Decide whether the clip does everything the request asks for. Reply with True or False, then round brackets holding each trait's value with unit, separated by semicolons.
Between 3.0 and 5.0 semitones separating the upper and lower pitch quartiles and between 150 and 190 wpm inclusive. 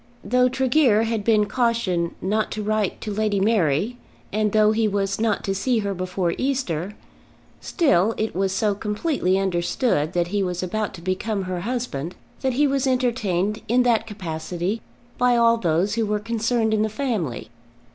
True (3.8 semitones; 170 wpm)